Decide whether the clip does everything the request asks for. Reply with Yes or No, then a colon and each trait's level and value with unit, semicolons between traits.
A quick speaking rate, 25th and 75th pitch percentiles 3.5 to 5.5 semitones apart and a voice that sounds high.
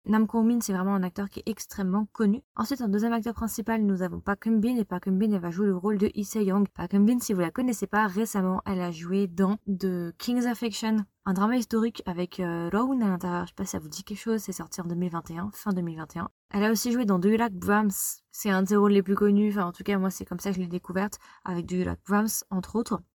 No: fast, 265 wpm; average, 2.8 semitones; high, 200 Hz